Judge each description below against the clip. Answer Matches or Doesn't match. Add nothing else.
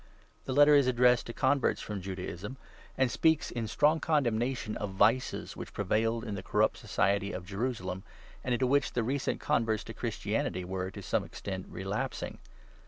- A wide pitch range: Doesn't match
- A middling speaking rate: Matches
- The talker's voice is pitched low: Matches